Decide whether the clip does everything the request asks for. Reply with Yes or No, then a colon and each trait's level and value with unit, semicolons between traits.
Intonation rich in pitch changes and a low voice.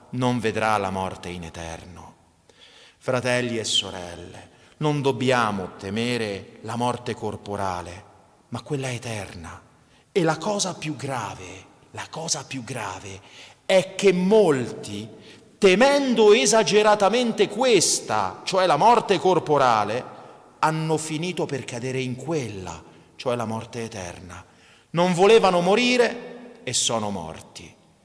Yes: wide, 8.9 semitones; low, 125 Hz